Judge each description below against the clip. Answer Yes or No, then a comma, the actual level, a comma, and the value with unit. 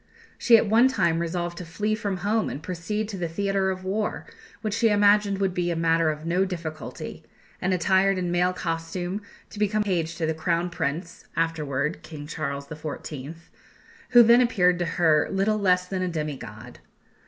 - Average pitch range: Yes, average, 3.5 semitones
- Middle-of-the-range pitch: Yes, medium, 180 Hz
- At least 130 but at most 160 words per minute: No, average, 185 wpm